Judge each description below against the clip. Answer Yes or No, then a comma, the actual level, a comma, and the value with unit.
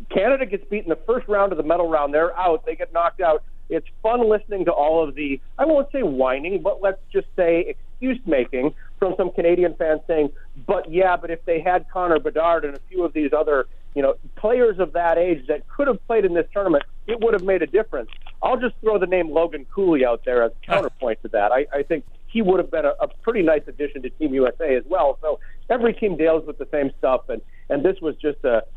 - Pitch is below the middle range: No, medium, 170 Hz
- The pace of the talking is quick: Yes, fast, 240 wpm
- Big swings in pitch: Yes, wide, 5.7 semitones